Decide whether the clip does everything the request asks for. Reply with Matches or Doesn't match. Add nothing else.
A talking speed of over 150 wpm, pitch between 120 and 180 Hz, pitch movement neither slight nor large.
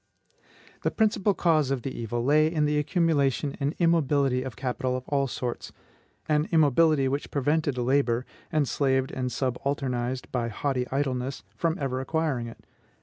Doesn't match